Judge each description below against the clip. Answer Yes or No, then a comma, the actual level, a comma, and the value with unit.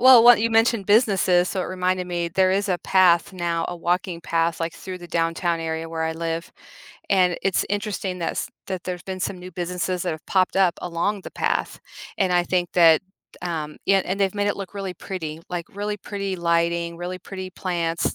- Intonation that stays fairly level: Yes, narrow, 2.3 semitones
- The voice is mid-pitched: Yes, medium, 180 Hz